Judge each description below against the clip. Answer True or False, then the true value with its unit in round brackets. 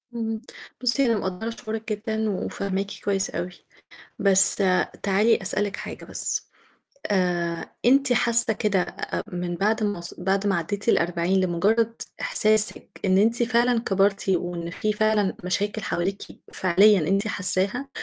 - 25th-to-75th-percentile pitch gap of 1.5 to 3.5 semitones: True (2.9 semitones)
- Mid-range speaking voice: False (200 Hz)